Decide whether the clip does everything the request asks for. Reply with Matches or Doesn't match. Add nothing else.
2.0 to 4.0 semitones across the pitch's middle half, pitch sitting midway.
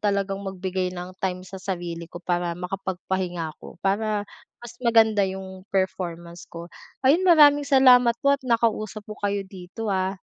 Doesn't match